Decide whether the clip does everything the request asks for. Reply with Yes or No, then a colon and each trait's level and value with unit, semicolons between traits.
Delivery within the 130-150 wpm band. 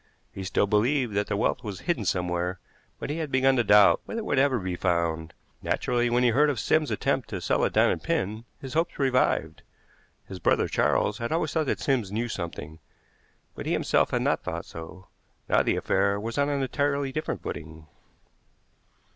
No: average, 195 wpm